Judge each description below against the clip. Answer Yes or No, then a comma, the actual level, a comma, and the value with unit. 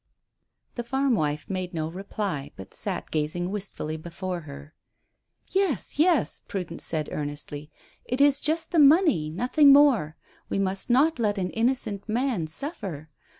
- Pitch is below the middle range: No, high, 195 Hz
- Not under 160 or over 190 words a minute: No, average, 145 wpm